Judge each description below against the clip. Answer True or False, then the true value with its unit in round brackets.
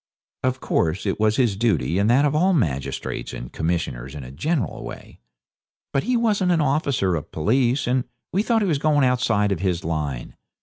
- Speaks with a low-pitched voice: True (120 Hz)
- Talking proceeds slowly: False (190 wpm)